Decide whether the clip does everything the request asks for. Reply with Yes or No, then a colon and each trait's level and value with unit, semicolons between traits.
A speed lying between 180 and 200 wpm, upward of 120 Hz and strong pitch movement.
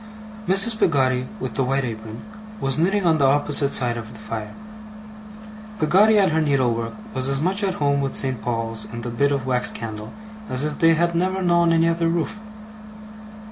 Yes: average, 185 wpm; medium, 140 Hz; wide, 6.0 semitones